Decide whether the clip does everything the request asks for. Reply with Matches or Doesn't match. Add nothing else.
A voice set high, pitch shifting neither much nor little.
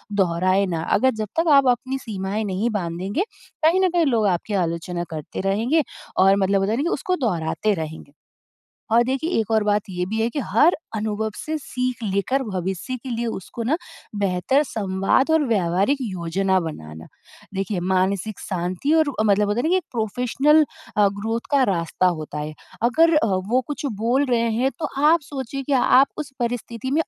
Doesn't match